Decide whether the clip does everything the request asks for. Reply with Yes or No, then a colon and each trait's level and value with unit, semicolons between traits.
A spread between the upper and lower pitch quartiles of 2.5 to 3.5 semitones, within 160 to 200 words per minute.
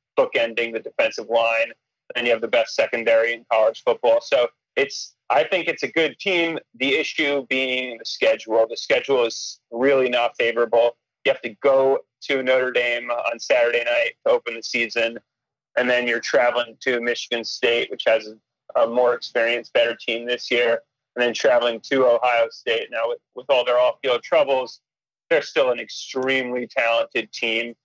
No: average, 4.2 semitones; average, 180 wpm